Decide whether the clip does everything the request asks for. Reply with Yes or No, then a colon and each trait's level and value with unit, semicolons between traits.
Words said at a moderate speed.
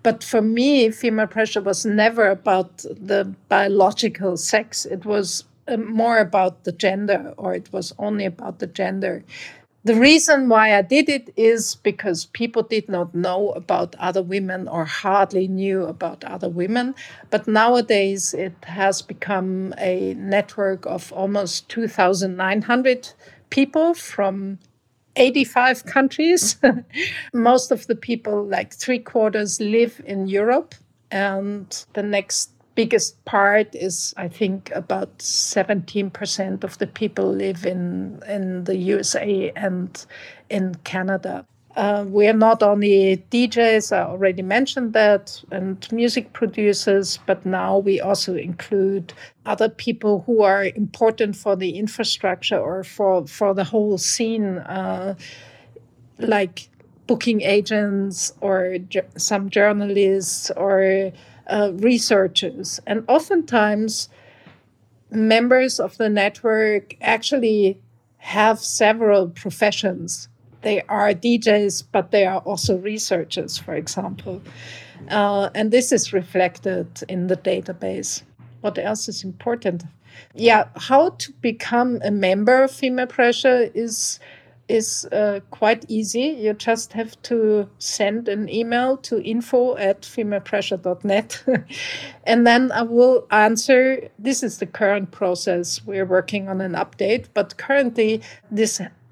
No: slow, 125 wpm